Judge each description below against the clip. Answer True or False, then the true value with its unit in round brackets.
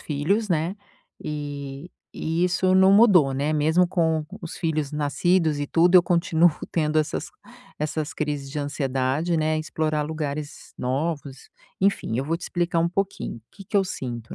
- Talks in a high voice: False (155 Hz)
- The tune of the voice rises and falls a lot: False (3.2 semitones)